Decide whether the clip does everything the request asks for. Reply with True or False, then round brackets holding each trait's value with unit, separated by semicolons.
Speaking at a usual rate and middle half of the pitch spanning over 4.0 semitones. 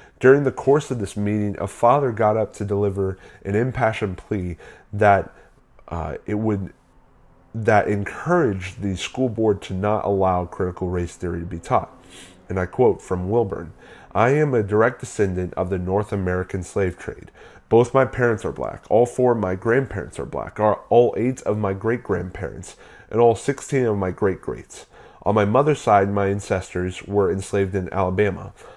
False (175 wpm; 3.3 semitones)